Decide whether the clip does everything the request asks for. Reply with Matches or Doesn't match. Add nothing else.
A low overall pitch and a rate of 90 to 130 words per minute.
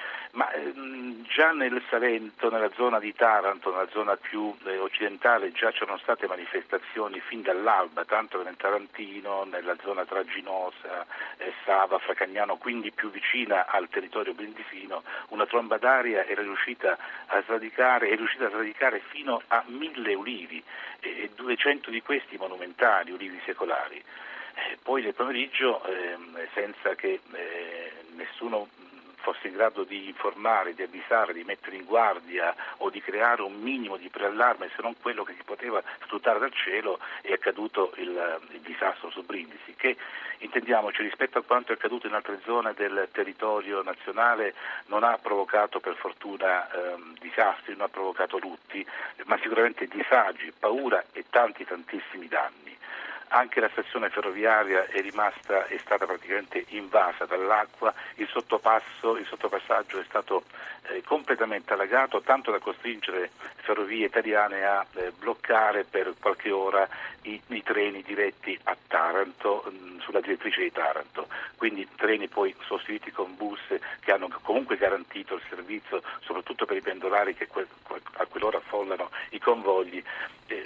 Doesn't match